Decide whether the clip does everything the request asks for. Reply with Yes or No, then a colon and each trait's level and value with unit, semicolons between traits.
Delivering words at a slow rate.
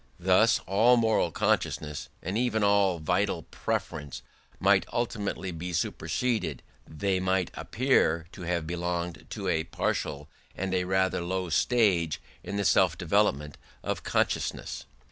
Yes: slow, 125 wpm